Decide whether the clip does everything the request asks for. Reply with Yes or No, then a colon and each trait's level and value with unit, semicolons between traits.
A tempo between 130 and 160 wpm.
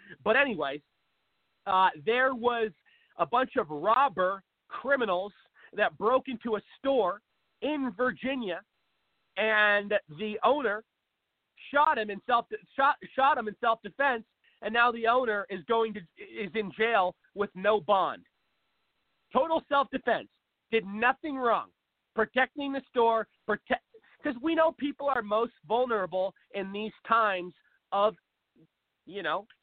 Yes: slow, 135 wpm